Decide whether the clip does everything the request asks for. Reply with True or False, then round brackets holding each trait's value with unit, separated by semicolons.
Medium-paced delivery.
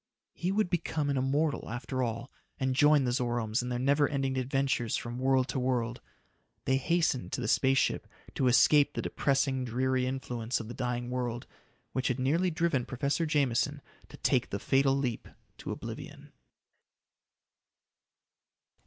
True (155 wpm)